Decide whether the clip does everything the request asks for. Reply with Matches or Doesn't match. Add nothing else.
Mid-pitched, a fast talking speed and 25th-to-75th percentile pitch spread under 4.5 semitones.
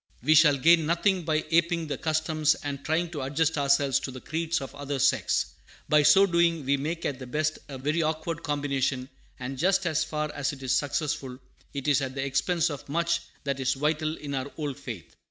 Matches